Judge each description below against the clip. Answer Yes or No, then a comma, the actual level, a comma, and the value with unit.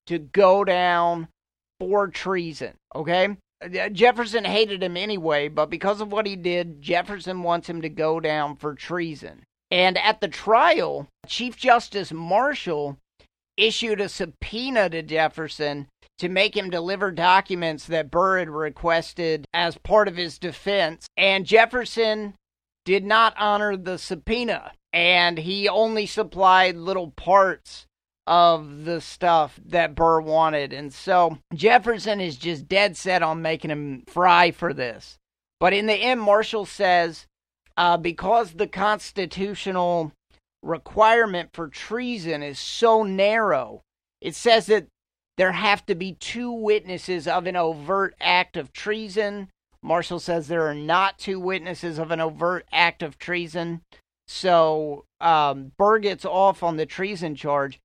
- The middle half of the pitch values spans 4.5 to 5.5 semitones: No, average, 3.8 semitones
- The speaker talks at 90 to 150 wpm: Yes, average, 140 wpm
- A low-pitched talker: No, medium, 180 Hz